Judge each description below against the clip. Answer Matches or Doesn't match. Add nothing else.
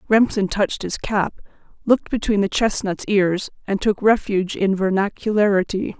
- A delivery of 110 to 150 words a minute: Matches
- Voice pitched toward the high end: Matches